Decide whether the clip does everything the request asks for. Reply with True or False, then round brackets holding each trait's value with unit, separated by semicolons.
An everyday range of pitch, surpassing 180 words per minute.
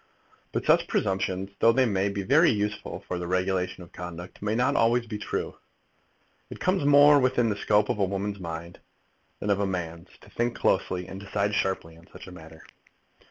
True (3.6 semitones; 200 wpm)